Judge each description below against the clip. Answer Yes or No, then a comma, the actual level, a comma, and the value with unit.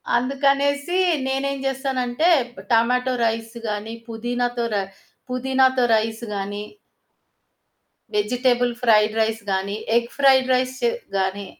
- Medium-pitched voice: No, high, 245 Hz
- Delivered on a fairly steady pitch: No, average, 3.1 semitones